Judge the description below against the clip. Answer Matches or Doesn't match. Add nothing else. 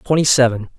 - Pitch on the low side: Matches